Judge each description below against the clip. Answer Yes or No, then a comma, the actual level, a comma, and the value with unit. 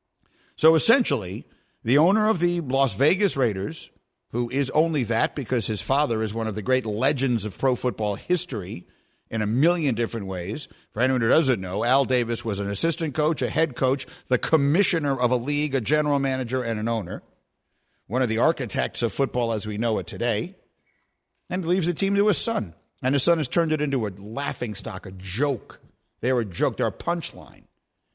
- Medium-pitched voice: No, low, 130 Hz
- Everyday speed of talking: Yes, average, 195 wpm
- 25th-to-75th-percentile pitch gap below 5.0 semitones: No, average, 5.3 semitones